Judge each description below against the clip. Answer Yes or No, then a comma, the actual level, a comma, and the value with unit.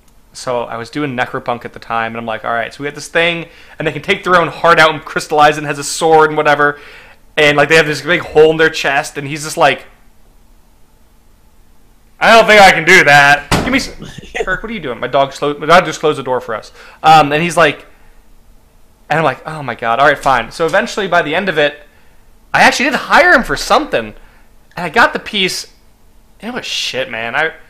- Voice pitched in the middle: Yes, medium, 150 Hz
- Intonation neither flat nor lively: Yes, average, 3.1 semitones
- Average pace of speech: No, fast, 240 wpm